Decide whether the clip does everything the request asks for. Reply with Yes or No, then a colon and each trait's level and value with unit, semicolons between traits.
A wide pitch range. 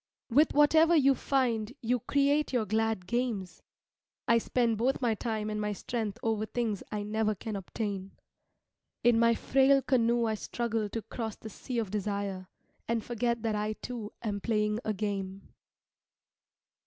No: narrow, 2.4 semitones